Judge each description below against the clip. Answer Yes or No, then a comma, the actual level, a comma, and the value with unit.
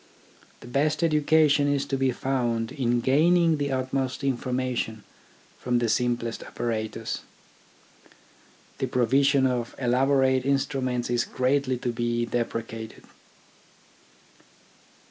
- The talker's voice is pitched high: No, low, 130 Hz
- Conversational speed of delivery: No, slow, 110 wpm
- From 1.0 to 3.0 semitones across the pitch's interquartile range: Yes, narrow, 2.6 semitones